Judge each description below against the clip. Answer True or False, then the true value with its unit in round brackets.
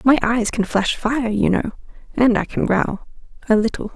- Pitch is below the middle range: False (225 Hz)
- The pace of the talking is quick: False (180 wpm)